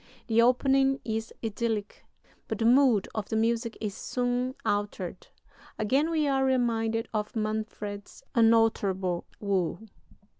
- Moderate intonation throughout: Yes, average, 3.0 semitones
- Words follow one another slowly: Yes, slow, 120 wpm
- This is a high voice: Yes, high, 225 Hz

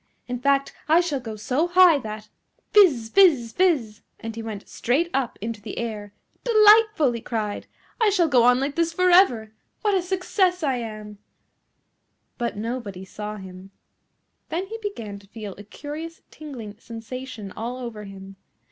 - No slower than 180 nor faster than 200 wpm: No, average, 165 wpm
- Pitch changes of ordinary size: No, wide, 7.8 semitones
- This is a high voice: Yes, high, 245 Hz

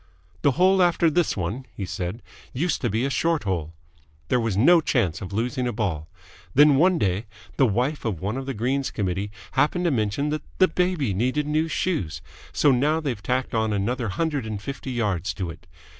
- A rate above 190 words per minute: Yes, average, 200 wpm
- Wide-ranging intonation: Yes, wide, 6.7 semitones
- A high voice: No, low, 125 Hz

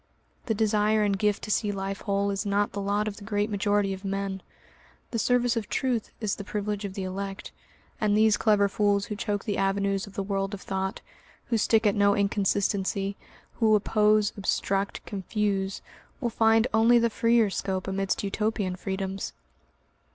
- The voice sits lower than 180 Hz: No, high, 205 Hz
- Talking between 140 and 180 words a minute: Yes, average, 175 wpm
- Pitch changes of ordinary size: No, narrow, 1.5 semitones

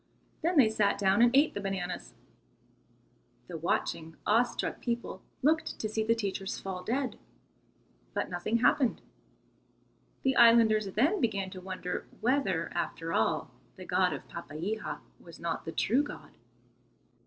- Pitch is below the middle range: No, high, 215 Hz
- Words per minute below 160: Yes, average, 140 wpm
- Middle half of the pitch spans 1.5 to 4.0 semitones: No, average, 4.7 semitones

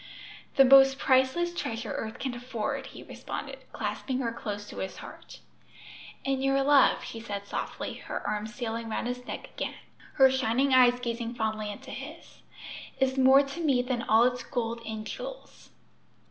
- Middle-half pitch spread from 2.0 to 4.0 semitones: Yes, average, 3.0 semitones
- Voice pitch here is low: No, very high, 250 Hz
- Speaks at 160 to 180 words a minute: Yes, average, 165 wpm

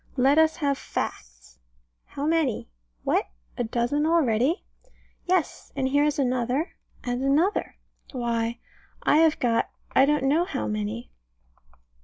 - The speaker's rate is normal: No, slow, 130 wpm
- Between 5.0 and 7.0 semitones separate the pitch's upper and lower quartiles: No, average, 4.3 semitones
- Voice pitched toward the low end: No, very high, 270 Hz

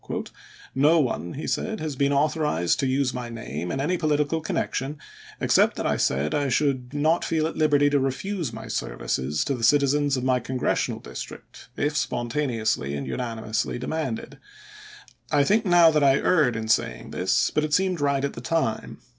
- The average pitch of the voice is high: No, medium, 140 Hz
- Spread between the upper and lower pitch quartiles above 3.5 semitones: Yes, average, 4.6 semitones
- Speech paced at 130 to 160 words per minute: No, average, 180 wpm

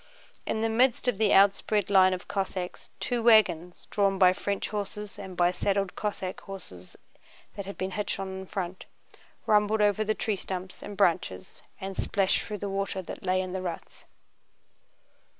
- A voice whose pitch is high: Yes, high, 195 Hz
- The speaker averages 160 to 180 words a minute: Yes, average, 170 wpm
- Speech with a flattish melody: Yes, narrow, 1.9 semitones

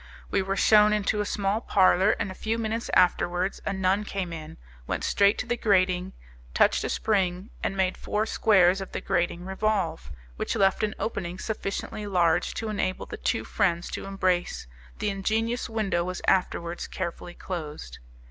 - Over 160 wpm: Yes, average, 170 wpm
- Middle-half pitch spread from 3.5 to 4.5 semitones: No, average, 2.8 semitones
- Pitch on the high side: Yes, high, 195 Hz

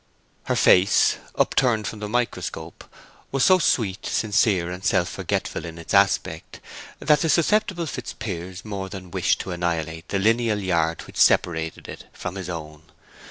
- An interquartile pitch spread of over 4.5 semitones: Yes, average, 4.9 semitones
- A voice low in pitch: Yes, very low, 95 Hz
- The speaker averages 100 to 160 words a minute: Yes, average, 155 wpm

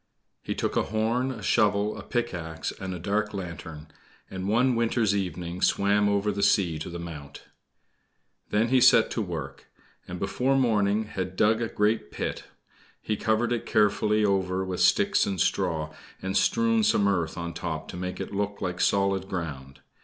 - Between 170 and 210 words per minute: Yes, average, 175 wpm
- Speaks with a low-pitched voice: Yes, low, 100 Hz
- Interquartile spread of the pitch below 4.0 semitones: Yes, average, 3.6 semitones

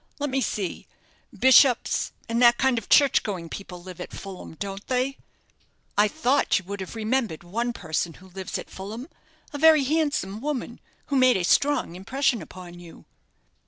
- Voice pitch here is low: No, high, 225 Hz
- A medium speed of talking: Yes, average, 170 wpm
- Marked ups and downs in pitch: Yes, wide, 5.9 semitones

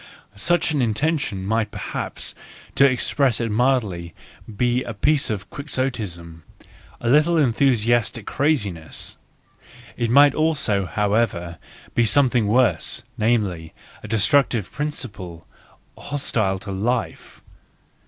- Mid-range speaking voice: No, low, 115 Hz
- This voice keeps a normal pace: No, slow, 105 wpm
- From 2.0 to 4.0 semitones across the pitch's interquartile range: No, average, 5.3 semitones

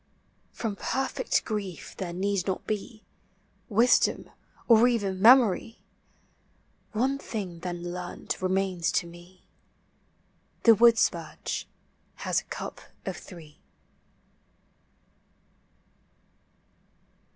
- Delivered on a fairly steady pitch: No, average, 4.1 semitones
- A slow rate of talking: Yes, slow, 85 wpm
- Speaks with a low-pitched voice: No, high, 195 Hz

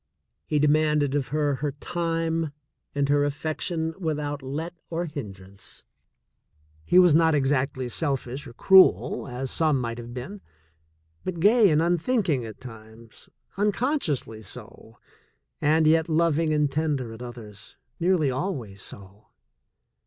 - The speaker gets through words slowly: Yes, slow, 130 wpm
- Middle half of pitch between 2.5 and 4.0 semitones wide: No, average, 4.6 semitones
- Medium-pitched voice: Yes, medium, 145 Hz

